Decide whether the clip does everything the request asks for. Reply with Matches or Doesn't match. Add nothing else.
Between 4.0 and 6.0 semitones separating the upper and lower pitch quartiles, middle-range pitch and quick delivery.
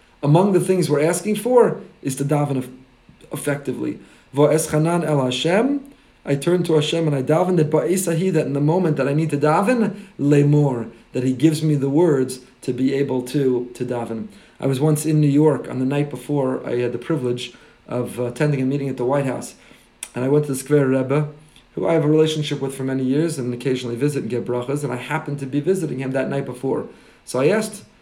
Doesn't match